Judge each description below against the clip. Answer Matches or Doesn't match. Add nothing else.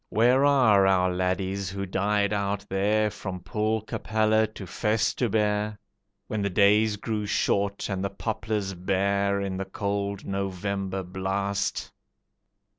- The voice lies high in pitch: Doesn't match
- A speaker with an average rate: Doesn't match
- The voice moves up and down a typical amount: Doesn't match